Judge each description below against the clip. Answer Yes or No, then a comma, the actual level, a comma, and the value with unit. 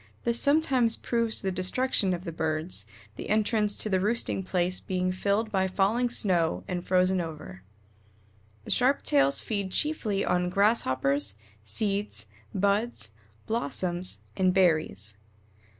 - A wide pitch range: No, average, 3.9 semitones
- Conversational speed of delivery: No, slow, 130 wpm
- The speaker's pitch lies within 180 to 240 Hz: Yes, high, 190 Hz